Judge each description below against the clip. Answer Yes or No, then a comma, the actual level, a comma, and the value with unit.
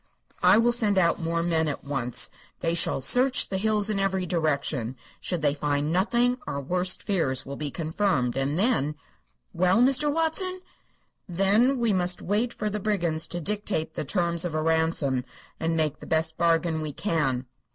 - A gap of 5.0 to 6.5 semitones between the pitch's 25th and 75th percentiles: Yes, wide, 5.4 semitones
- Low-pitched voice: No, medium, 170 Hz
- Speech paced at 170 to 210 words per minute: Yes, average, 180 wpm